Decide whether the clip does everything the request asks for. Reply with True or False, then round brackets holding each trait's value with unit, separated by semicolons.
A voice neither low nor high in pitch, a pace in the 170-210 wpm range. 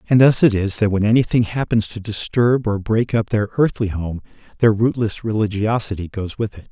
False (110 Hz; 195 wpm)